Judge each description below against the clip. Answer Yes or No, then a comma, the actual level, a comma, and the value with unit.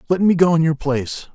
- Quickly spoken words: Yes, fast, 270 wpm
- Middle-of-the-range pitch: Yes, medium, 160 Hz